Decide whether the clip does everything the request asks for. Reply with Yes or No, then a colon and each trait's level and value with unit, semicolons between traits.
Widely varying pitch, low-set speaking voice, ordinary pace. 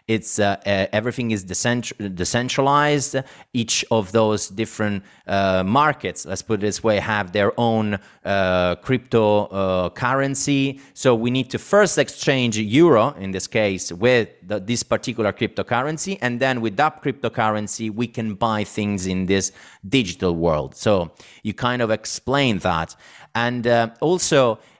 No: average, 4.0 semitones; low, 115 Hz; average, 150 wpm